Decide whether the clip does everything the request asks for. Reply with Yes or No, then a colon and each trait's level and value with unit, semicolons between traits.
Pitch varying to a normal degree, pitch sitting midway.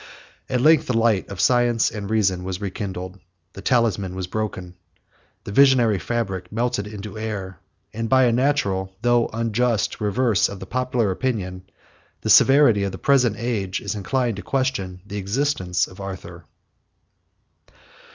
No: average, 4.2 semitones; low, 105 Hz